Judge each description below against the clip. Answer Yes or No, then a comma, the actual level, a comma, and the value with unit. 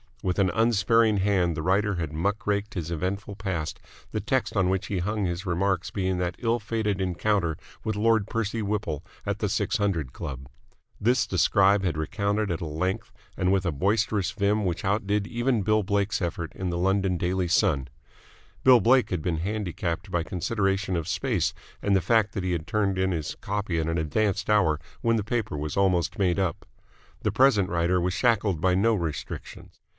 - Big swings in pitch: No, average, 3.2 semitones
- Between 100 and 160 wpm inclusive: No, average, 190 wpm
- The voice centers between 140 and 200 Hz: No, very low, 95 Hz